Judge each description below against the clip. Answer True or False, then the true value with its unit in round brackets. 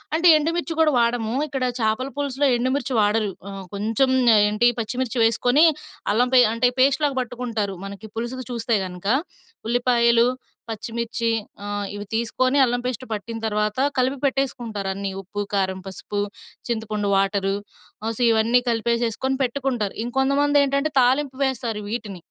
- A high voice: True (235 Hz)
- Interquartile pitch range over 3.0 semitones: True (3.5 semitones)